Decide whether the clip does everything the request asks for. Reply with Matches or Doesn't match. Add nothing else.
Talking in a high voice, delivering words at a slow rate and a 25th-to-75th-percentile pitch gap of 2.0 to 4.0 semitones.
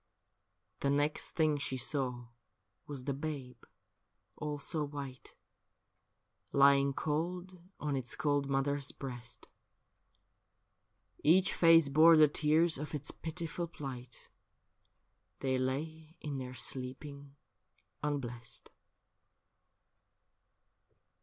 Doesn't match